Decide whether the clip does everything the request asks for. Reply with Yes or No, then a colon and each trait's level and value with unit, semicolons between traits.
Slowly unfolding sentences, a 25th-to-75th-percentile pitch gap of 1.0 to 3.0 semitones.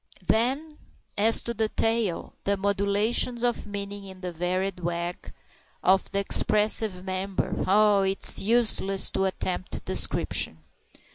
Yes: slow, 125 wpm; average, 2.7 semitones